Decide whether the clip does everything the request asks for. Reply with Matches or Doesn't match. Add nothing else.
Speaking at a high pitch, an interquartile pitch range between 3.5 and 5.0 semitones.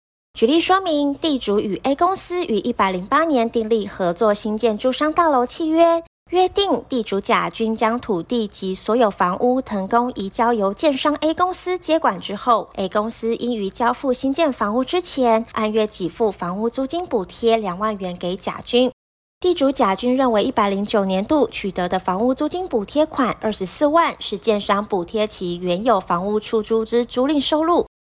Doesn't match